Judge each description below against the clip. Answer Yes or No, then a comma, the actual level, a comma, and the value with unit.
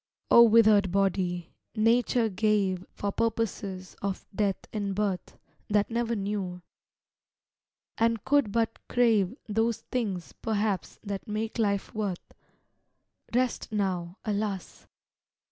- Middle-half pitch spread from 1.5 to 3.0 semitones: Yes, average, 2.7 semitones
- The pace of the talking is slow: Yes, slow, 110 wpm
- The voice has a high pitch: Yes, high, 210 Hz